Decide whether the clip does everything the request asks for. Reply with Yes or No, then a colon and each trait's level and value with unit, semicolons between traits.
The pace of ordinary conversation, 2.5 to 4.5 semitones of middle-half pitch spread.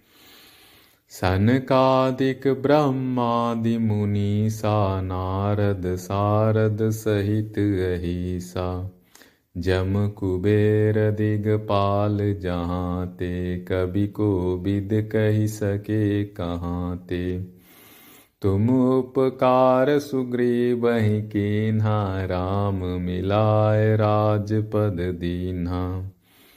No: slow, 65 wpm; average, 2.9 semitones